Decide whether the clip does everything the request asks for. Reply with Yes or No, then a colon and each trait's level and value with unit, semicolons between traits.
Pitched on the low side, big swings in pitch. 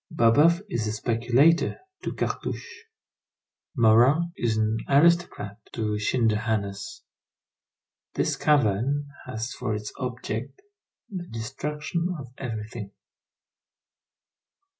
Yes: low, 120 Hz; wide, 5.9 semitones